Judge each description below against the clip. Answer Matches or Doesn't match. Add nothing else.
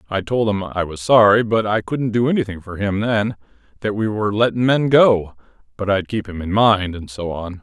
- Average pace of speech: Doesn't match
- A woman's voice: Doesn't match